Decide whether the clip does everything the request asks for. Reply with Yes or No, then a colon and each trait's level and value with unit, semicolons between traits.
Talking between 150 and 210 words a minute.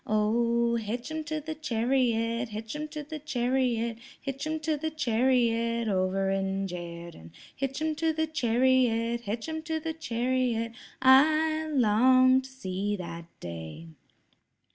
No: average, 140 wpm